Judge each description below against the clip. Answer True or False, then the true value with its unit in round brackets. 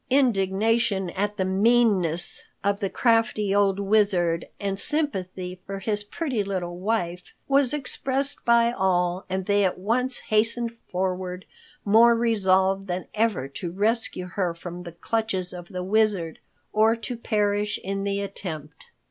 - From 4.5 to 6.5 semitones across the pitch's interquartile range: False (3.7 semitones)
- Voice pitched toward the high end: True (200 Hz)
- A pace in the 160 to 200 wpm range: False (140 wpm)